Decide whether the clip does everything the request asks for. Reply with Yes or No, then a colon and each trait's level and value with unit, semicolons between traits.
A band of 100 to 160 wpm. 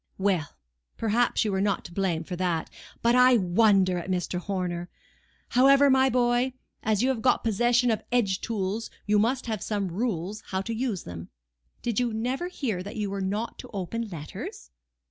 No: average, 185 wpm